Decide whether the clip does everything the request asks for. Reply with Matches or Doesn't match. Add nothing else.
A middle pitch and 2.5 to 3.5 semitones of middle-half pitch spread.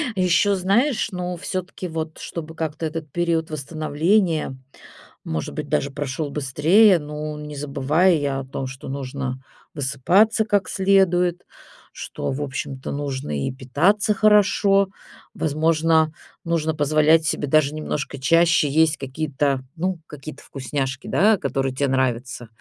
Doesn't match